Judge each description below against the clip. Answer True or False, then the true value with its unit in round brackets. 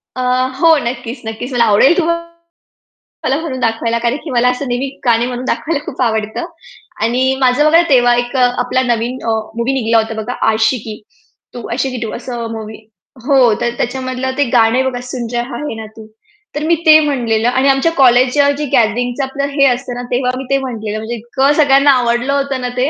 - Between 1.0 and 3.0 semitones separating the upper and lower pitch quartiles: True (2.6 semitones)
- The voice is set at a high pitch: True (250 Hz)